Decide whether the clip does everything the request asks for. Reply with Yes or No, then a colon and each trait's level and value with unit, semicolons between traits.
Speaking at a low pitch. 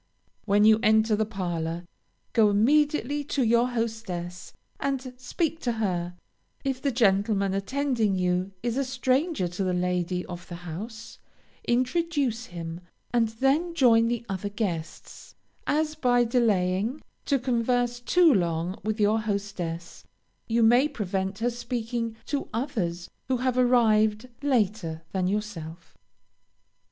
No: high, 225 Hz